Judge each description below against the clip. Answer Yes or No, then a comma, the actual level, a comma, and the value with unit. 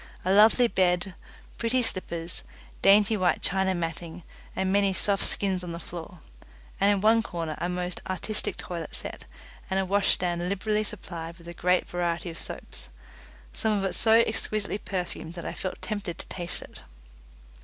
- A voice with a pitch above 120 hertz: Yes, medium, 185 Hz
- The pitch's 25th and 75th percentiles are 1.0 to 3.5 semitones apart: Yes, average, 2.7 semitones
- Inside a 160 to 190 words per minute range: Yes, average, 170 wpm